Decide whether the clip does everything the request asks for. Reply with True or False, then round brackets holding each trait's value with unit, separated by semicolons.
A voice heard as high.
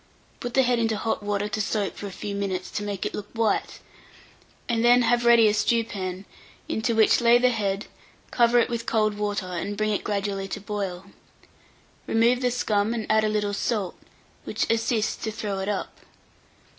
True (215 Hz)